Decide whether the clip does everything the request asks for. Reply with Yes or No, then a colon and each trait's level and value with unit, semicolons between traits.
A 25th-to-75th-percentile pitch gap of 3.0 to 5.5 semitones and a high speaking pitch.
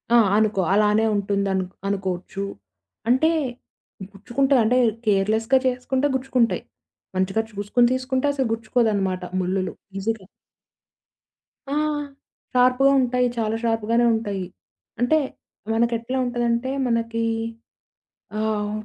Yes: average, 3.6 semitones; high, 225 Hz